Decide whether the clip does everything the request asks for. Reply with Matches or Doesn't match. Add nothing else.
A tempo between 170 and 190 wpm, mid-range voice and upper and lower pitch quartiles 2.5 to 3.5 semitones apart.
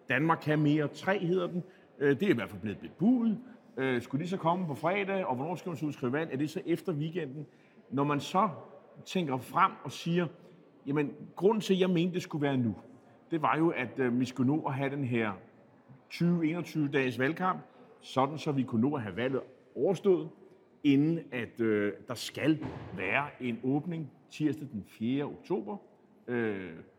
Doesn't match